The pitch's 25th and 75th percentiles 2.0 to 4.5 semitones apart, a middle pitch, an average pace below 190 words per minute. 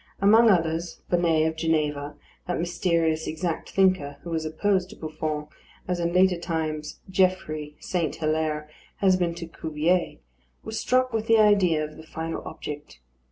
Yes: average, 2.9 semitones; medium, 165 Hz; average, 155 wpm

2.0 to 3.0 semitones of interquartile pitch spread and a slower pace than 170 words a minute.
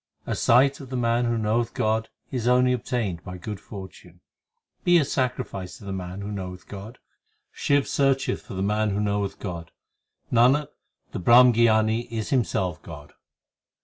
No: average, 4.3 semitones; average, 160 wpm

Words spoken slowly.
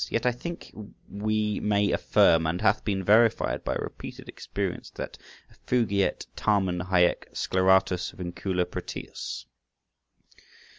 Yes: slow, 115 wpm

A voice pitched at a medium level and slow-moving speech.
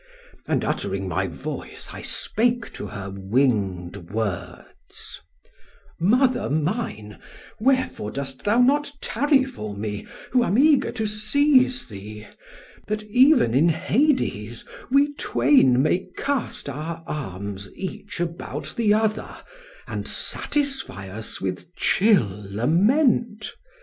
Yes: medium, 180 Hz; slow, 115 wpm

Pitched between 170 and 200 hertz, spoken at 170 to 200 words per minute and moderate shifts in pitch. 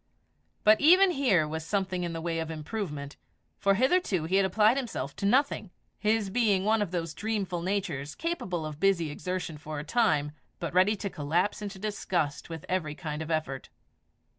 Yes: medium, 185 Hz; average, 180 wpm; average, 4.9 semitones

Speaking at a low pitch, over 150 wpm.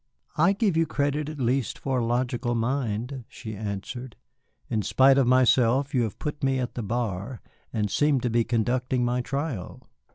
Yes: low, 125 Hz; average, 175 wpm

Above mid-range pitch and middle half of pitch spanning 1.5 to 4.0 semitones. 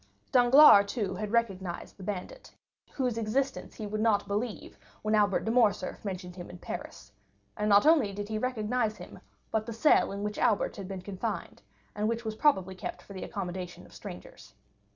Yes: high, 210 Hz; average, 2.9 semitones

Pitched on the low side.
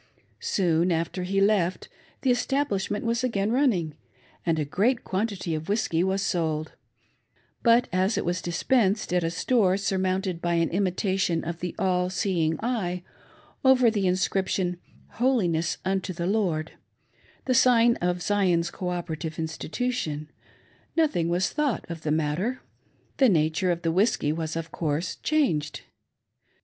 No: medium, 185 Hz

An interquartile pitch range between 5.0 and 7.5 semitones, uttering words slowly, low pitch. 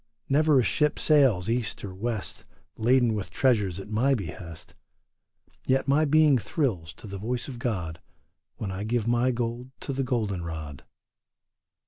No: average, 5.3 semitones; average, 155 wpm; low, 115 Hz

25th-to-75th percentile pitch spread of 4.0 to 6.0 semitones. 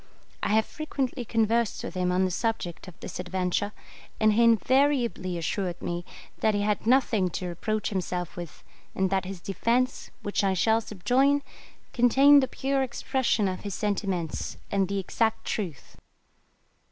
Yes: average, 4.4 semitones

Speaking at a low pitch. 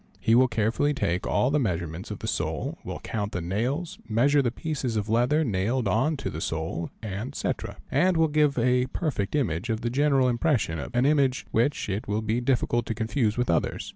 Yes: low, 120 Hz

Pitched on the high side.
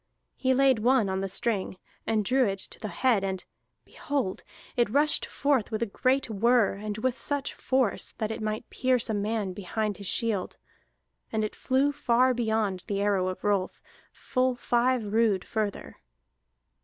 Yes: high, 220 Hz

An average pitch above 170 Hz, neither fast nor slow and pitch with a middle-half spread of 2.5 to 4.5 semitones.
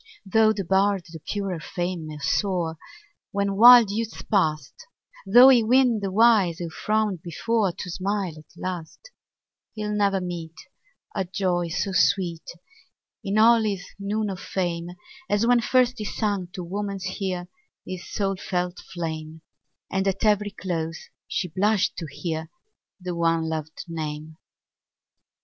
Yes: high, 190 Hz; average, 145 wpm; average, 3.7 semitones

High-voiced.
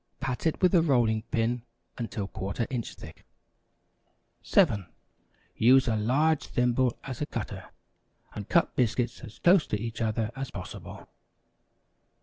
No: low, 120 Hz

